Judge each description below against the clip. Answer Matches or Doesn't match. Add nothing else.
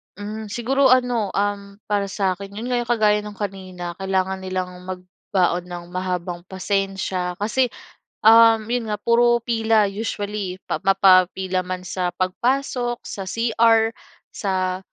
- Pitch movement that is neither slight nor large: Matches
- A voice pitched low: Doesn't match